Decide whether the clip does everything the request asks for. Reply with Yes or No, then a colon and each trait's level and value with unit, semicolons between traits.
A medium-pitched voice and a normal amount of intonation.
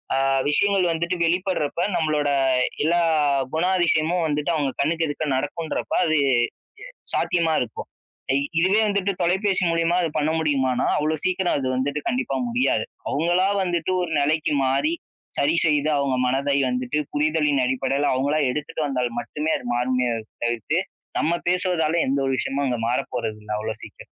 Yes: medium, 150 Hz; average, 4.1 semitones